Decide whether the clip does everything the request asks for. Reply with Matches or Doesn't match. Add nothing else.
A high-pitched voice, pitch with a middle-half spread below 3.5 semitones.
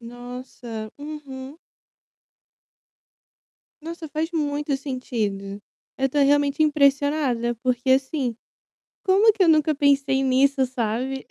Matches